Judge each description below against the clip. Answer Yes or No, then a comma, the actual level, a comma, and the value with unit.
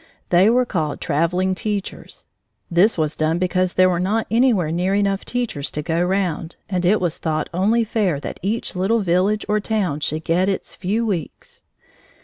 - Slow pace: No, average, 175 wpm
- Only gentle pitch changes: No, average, 3.7 semitones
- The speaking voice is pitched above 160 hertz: Yes, medium, 185 Hz